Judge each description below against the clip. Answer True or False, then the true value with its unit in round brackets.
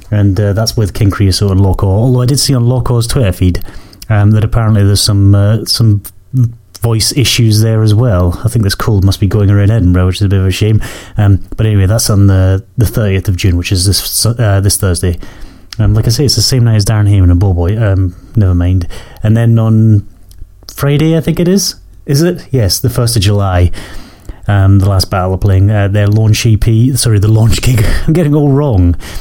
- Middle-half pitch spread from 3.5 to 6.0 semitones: False (2.9 semitones)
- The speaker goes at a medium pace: False (225 wpm)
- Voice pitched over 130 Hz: False (105 Hz)